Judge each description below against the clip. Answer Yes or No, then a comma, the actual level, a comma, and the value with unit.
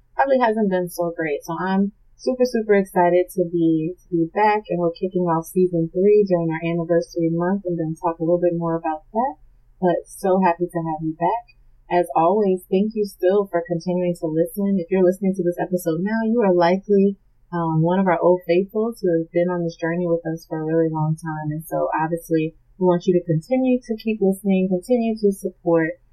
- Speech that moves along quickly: Yes, fast, 215 wpm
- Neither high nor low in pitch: Yes, medium, 175 Hz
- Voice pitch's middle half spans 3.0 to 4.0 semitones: No, narrow, 2.6 semitones